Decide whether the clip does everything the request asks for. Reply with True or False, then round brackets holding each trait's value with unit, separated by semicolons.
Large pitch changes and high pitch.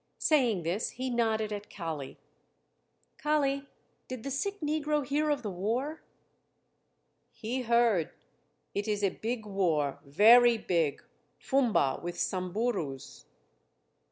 True (6.4 semitones; 225 Hz)